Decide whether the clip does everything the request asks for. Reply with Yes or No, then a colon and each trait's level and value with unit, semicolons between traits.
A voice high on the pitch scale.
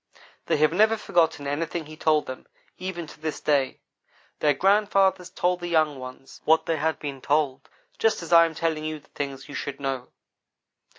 No: medium, 155 Hz